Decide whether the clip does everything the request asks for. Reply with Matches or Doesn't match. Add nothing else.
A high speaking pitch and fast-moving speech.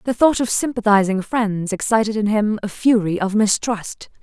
Doesn't match